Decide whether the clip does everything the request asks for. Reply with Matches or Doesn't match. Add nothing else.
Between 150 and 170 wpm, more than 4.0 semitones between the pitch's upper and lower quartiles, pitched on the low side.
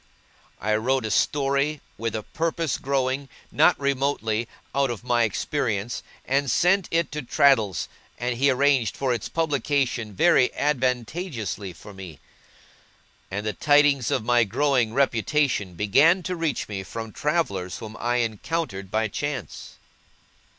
Doesn't match